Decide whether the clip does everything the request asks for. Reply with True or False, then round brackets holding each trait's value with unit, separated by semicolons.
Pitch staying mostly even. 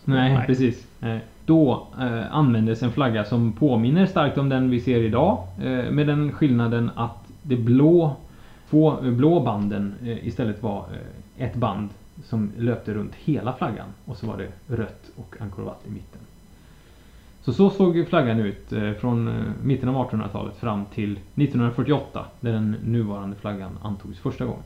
False (3.7 semitones)